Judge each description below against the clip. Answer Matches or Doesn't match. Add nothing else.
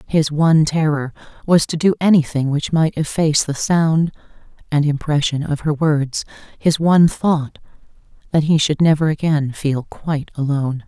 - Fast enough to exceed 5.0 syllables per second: Doesn't match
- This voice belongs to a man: Doesn't match